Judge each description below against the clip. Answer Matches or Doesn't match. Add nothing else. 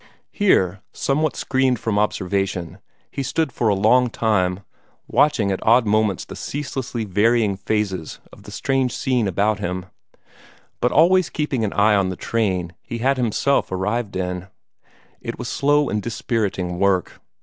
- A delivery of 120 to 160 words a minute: Matches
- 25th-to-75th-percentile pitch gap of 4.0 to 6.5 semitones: Matches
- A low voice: Matches